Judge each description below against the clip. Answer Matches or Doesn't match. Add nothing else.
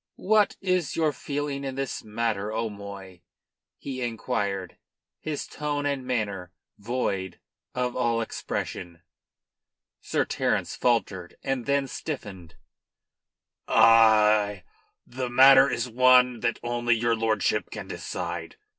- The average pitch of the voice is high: Doesn't match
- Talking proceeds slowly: Matches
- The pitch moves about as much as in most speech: Matches